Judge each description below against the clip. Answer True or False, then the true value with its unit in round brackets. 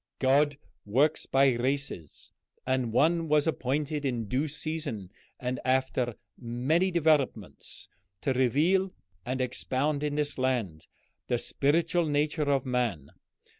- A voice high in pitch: False (135 Hz)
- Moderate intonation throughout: True (3.3 semitones)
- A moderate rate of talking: False (120 wpm)